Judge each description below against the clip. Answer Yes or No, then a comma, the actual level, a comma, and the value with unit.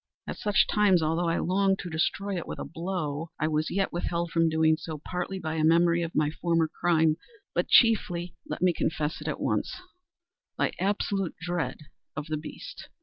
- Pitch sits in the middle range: Yes, medium, 170 Hz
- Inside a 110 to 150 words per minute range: No, average, 180 wpm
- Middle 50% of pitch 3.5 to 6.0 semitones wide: No, average, 3.1 semitones